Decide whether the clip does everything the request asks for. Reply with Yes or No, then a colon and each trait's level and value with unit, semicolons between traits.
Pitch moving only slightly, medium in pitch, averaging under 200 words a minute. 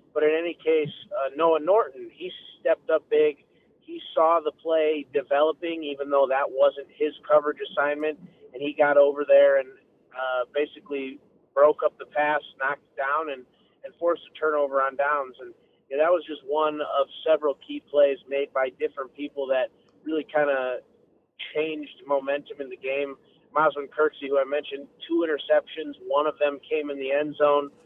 Yes: narrow, 2.1 semitones; medium, 150 Hz; average, 180 wpm